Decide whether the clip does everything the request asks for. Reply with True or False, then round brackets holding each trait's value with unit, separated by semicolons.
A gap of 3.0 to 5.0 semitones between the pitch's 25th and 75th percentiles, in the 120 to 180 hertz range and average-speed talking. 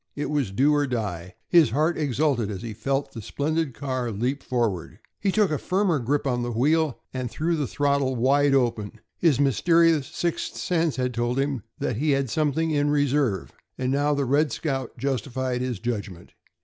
True (3.6 semitones; 135 Hz; 185 wpm)